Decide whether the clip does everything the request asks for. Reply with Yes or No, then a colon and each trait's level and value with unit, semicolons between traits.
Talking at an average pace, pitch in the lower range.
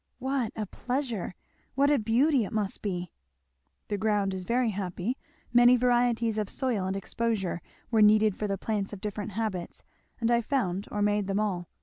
No: average, 180 wpm; high, 215 Hz